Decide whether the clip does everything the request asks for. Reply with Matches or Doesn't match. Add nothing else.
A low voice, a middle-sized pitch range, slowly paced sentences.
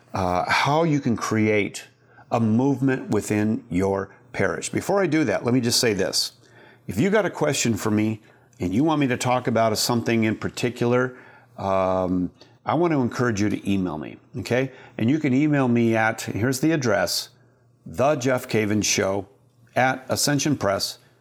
Doesn't match